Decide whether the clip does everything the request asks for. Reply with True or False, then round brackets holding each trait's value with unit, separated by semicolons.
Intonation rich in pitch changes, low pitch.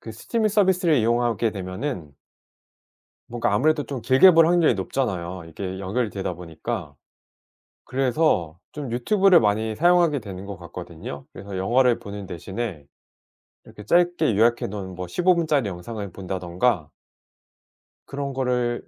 True (7.1 semitones; 115 Hz)